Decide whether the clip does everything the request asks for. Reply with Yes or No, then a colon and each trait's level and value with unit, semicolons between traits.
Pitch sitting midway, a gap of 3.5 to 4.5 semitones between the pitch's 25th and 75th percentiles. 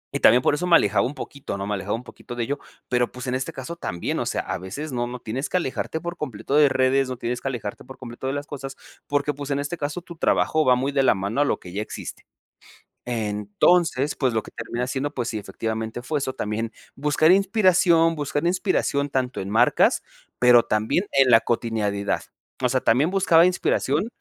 No: low, 130 Hz; average, 4.2 semitones